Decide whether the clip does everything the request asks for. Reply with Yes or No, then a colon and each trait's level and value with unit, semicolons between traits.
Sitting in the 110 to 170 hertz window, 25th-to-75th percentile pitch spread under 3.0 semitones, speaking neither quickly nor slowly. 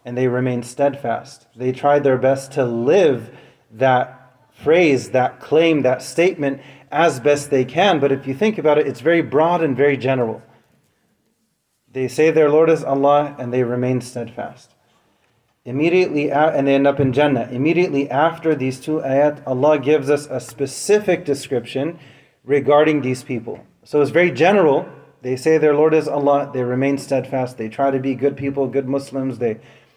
Yes: medium, 140 Hz; narrow, 2.6 semitones; average, 170 wpm